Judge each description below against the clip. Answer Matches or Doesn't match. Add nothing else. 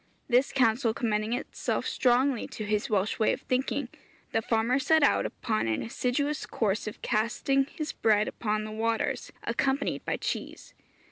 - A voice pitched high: Matches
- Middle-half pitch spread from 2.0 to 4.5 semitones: Matches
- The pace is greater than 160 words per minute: Doesn't match